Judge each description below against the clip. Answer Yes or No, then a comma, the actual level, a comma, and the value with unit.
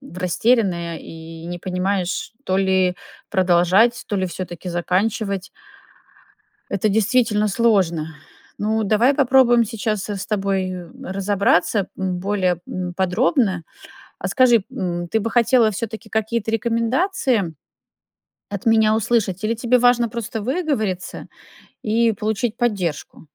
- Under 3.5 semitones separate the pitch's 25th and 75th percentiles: No, average, 3.9 semitones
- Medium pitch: No, high, 205 Hz